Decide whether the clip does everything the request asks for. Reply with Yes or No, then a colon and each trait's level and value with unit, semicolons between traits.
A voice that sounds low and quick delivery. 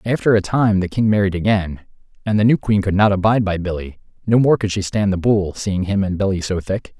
Yes: low, 100 Hz; fast, 240 wpm